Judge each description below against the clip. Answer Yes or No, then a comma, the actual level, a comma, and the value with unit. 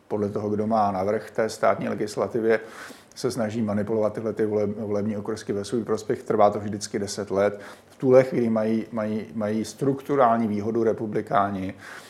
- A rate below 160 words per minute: No, average, 165 wpm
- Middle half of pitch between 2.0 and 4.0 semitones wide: No, narrow, 1.4 semitones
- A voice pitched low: Yes, low, 110 Hz